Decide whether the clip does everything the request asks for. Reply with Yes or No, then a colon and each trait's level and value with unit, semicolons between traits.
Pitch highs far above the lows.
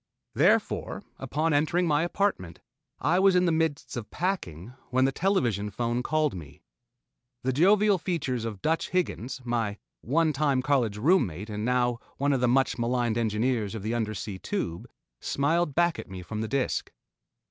Yes: wide, 6.7 semitones